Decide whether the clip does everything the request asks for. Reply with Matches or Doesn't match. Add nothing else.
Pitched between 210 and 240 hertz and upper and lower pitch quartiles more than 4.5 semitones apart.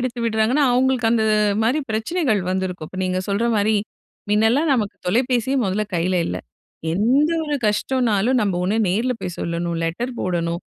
Matches